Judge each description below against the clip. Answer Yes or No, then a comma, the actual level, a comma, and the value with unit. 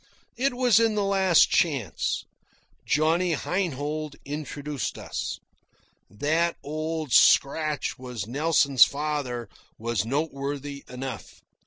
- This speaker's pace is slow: Yes, slow, 100 wpm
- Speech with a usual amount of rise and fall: Yes, average, 3.4 semitones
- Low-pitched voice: No, medium, 150 Hz